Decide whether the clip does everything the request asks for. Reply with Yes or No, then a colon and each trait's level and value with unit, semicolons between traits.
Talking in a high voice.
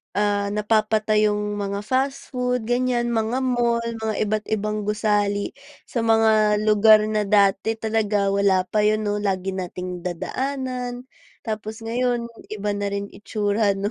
Yes: high, 215 Hz